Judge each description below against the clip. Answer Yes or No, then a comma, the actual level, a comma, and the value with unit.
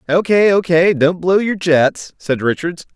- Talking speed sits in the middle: Yes, average, 160 wpm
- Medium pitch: Yes, medium, 175 Hz